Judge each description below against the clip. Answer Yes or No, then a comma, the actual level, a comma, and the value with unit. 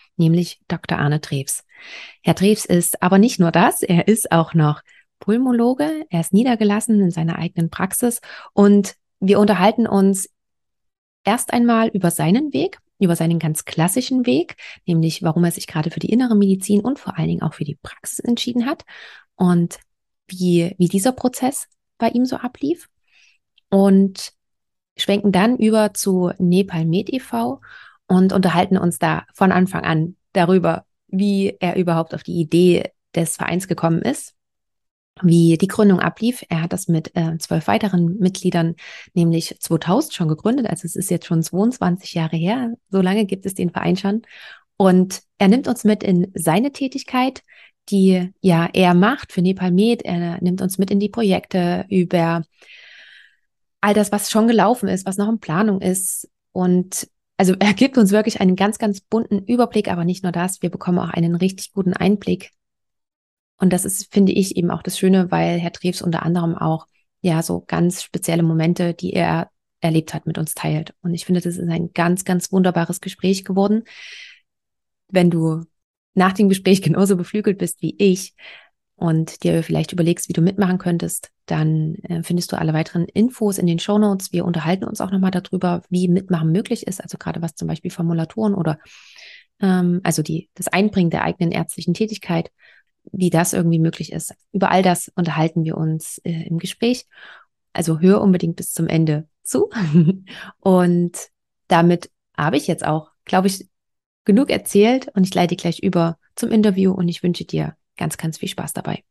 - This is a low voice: No, medium, 185 Hz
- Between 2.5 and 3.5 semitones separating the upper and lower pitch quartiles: Yes, average, 3.1 semitones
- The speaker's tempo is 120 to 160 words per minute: No, average, 175 wpm